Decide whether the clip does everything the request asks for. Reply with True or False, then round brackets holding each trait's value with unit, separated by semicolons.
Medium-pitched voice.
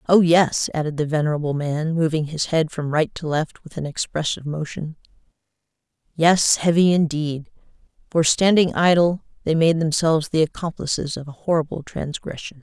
True (160 Hz)